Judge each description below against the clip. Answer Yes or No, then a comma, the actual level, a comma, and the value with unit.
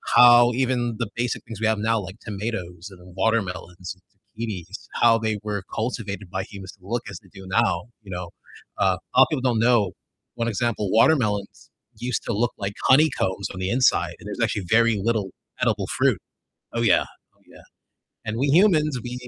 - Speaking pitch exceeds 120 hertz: No, low, 110 Hz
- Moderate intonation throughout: Yes, average, 3.9 semitones